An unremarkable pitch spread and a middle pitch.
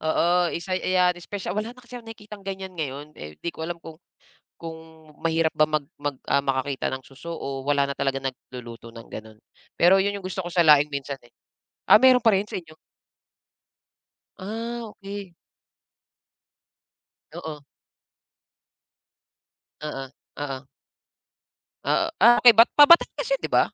No: wide, 6.1 semitones; medium, 165 Hz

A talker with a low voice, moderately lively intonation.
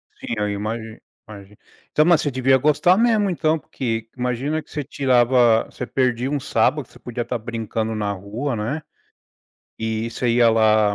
Yes: low, 120 Hz; average, 4.3 semitones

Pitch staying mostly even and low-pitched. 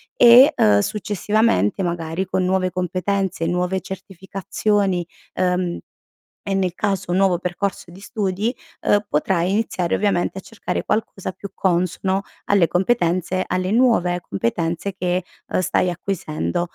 No: narrow, 2.1 semitones; medium, 185 Hz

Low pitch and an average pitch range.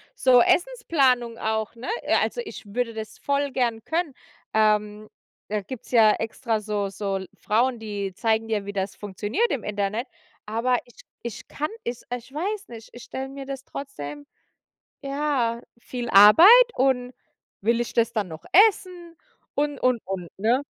No: high, 235 Hz; average, 4.0 semitones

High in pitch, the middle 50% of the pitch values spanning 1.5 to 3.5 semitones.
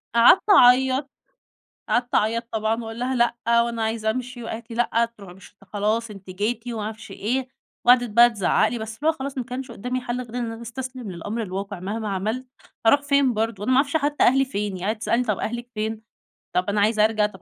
Yes: high, 230 Hz; average, 2.8 semitones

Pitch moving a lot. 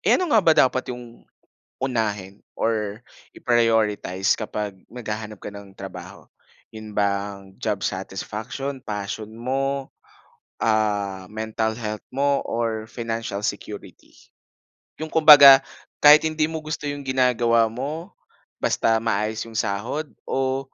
No: average, 4.3 semitones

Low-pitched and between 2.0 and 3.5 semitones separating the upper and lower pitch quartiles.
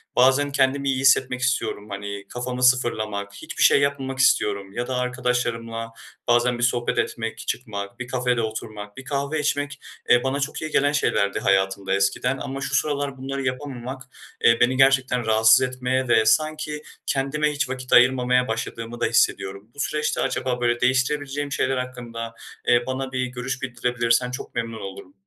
Yes: low, 125 Hz; average, 2.7 semitones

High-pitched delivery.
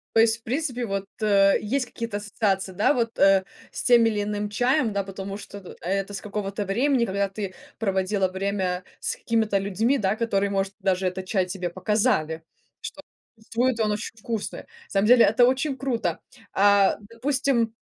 Yes: high, 205 Hz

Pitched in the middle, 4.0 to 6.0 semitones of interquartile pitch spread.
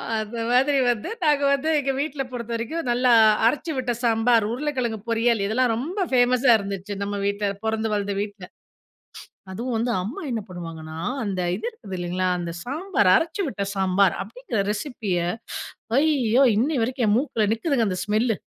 No: high, 230 Hz; average, 4.6 semitones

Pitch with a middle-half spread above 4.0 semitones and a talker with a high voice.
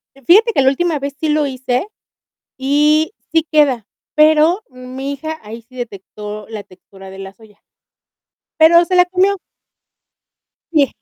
Yes: average, 5.3 semitones; very high, 280 Hz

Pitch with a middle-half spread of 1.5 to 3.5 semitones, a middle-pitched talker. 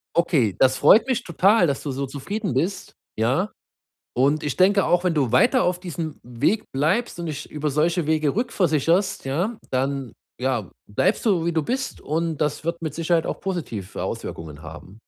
No: average, 5.3 semitones; medium, 160 Hz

